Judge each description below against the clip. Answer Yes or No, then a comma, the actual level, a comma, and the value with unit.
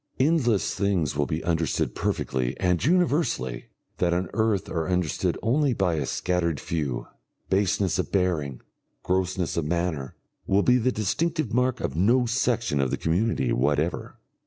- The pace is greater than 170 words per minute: No, average, 150 wpm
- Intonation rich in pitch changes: Yes, wide, 6.3 semitones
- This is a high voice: No, very low, 90 Hz